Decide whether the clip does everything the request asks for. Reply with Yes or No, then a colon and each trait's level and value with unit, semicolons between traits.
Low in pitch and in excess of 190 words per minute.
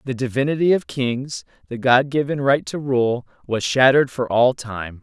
No: low, 130 Hz; average, 180 wpm